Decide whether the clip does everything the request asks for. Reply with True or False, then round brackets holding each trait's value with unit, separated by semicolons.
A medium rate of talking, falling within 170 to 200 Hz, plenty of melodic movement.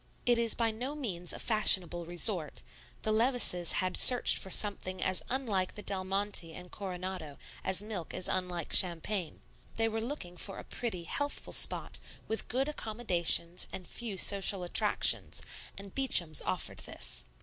False (155 wpm; 190 Hz; 4.1 semitones)